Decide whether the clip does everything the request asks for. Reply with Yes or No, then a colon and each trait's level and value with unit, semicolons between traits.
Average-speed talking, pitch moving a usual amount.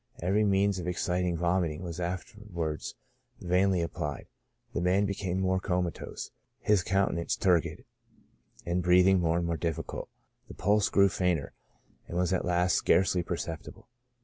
No: average, 150 wpm; narrow, 1.7 semitones